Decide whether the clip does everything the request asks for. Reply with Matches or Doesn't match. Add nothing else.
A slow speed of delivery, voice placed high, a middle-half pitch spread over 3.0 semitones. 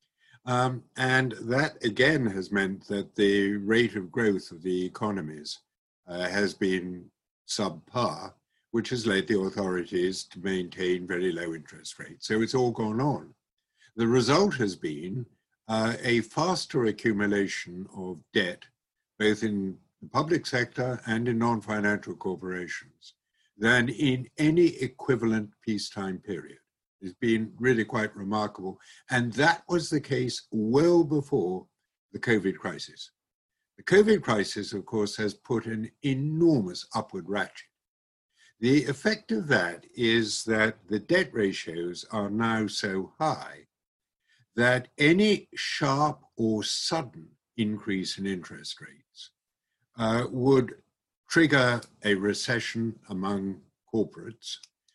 Doesn't match